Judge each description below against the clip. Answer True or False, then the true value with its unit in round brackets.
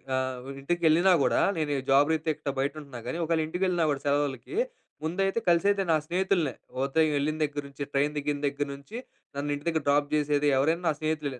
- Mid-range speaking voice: True (150 Hz)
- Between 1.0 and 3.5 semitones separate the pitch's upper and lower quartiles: True (2.8 semitones)